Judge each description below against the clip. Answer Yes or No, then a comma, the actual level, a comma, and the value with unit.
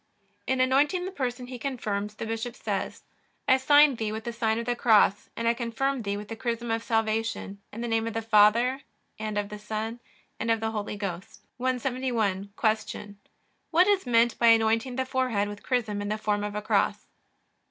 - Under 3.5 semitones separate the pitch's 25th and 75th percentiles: Yes, average, 2.9 semitones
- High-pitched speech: Yes, high, 225 Hz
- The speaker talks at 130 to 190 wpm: No, average, 200 wpm